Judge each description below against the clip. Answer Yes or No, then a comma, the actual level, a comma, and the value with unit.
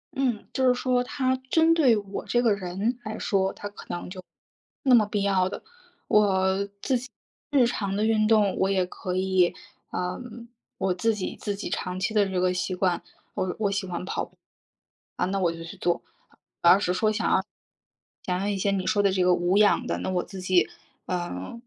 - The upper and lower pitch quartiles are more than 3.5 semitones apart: No, average, 3.0 semitones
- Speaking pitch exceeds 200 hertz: No, high, 195 Hz